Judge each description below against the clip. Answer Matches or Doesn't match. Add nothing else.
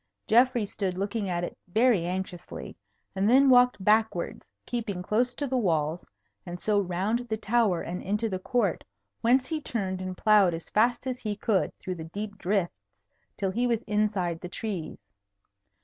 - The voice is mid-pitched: Doesn't match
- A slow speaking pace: Doesn't match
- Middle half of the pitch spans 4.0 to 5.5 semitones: Matches